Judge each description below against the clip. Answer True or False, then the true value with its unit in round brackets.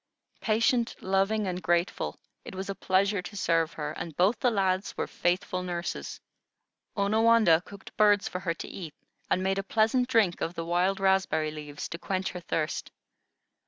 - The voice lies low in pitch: False (190 Hz)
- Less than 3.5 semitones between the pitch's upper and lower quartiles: True (2.9 semitones)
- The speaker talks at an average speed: True (170 wpm)